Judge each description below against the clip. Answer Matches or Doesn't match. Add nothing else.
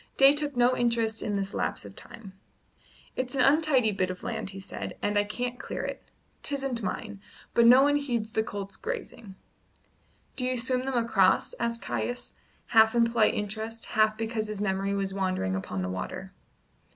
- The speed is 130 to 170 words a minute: Doesn't match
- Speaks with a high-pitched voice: Matches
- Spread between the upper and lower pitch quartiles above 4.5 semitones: Doesn't match